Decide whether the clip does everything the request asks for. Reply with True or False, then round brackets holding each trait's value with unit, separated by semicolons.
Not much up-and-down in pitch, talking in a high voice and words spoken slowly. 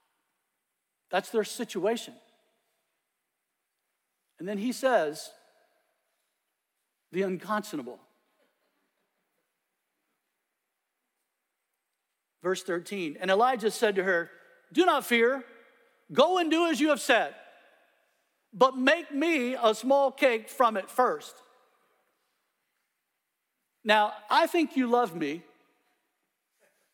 False (4.7 semitones; 235 Hz; 90 wpm)